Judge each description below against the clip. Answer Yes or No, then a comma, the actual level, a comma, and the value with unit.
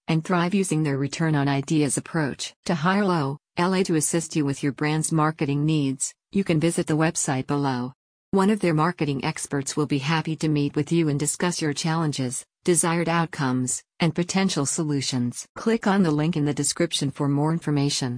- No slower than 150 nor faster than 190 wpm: Yes, average, 185 wpm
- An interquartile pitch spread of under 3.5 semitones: Yes, average, 2.9 semitones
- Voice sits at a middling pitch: Yes, medium, 155 Hz